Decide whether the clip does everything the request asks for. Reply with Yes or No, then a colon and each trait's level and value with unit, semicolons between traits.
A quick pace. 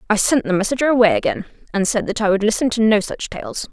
Yes: fast, 260 wpm